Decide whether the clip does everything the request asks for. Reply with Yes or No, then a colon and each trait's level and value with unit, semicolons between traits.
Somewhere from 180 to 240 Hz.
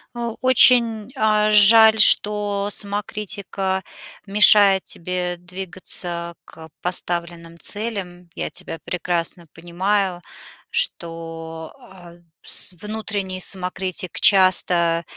Yes: medium, 185 Hz